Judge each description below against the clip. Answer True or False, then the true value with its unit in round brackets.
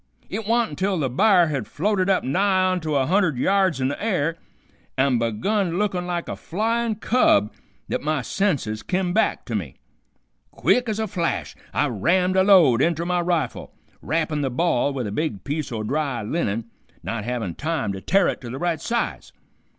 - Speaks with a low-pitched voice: False (165 Hz)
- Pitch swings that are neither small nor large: False (6.4 semitones)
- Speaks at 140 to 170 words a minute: False (190 wpm)